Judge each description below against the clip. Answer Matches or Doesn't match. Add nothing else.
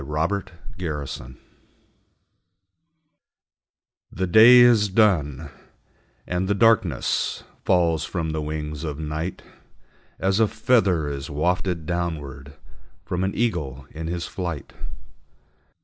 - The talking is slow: Matches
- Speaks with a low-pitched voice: Matches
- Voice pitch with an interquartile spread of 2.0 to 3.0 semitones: Doesn't match